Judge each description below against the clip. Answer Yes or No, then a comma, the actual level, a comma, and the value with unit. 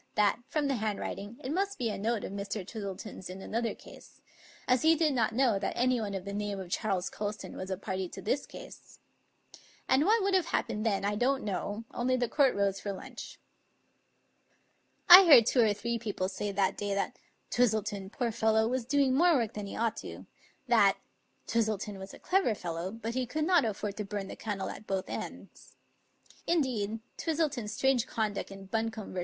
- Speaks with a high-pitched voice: Yes, high, 220 Hz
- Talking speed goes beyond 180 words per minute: Yes, average, 200 wpm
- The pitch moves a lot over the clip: No, average, 4.2 semitones